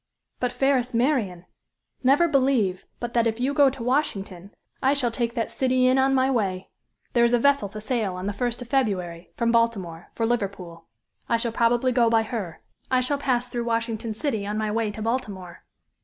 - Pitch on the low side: No, high, 235 Hz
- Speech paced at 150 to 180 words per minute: No, average, 200 wpm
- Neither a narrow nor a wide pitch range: Yes, average, 3.7 semitones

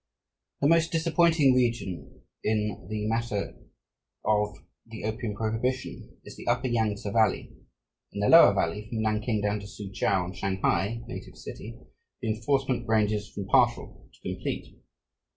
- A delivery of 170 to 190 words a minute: No, average, 140 wpm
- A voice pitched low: Yes, low, 110 Hz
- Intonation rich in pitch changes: No, narrow, 2.6 semitones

